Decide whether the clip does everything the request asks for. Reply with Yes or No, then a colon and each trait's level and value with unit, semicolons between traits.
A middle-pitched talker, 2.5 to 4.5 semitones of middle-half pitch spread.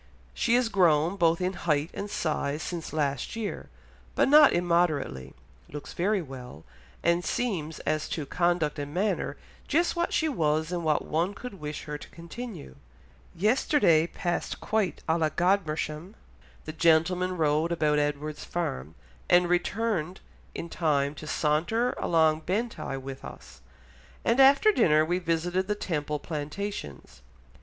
Yes: medium, 170 Hz; average, 4.2 semitones